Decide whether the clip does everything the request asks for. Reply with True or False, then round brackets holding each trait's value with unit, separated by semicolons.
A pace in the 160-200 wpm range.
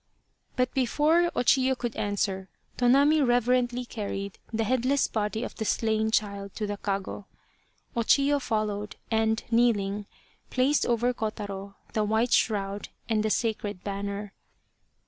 False (135 wpm)